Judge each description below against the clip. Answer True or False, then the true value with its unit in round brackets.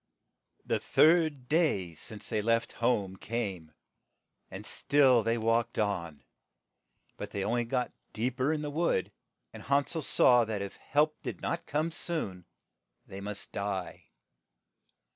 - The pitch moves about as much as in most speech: False (6.4 semitones)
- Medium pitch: False (115 Hz)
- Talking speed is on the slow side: False (145 wpm)